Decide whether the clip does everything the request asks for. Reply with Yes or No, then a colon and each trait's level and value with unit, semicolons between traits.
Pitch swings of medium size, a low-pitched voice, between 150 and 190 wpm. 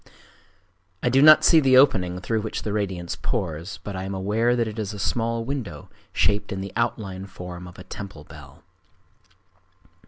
Yes: average, 4.2 semitones; low, 100 Hz; average, 180 wpm